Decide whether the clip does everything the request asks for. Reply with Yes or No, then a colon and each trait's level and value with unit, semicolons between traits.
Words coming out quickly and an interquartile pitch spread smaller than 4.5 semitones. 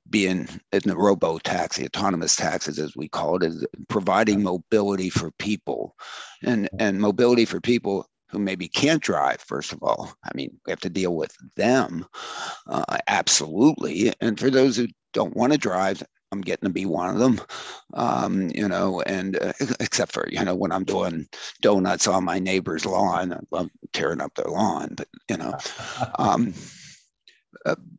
No: average, 175 wpm; average, 3.1 semitones